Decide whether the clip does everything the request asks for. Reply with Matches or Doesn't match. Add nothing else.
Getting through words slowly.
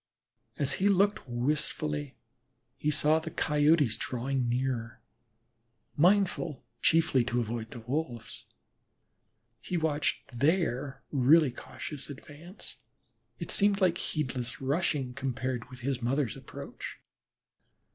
Matches